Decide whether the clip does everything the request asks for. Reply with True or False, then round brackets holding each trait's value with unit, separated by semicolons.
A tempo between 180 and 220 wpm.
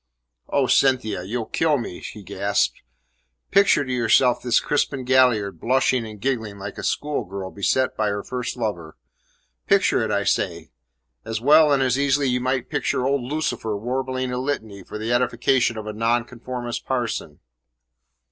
False (155 wpm)